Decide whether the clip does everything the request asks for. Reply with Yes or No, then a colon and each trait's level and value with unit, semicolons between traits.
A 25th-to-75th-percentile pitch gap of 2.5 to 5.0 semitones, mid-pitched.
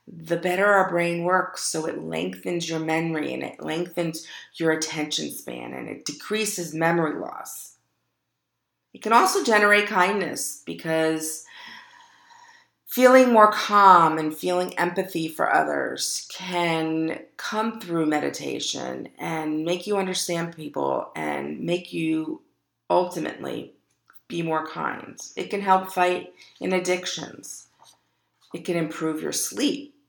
Yes: average, 4.2 semitones; medium, 175 Hz